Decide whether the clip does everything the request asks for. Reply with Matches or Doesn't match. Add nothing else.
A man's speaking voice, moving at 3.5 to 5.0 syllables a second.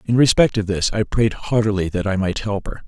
Doesn't match